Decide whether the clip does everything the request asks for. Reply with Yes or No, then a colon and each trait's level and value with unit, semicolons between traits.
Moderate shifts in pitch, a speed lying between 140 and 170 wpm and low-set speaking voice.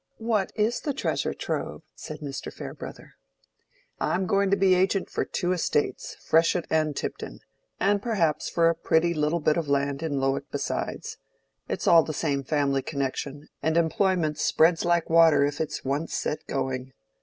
No: average, 3.8 semitones; average, 165 wpm; medium, 160 Hz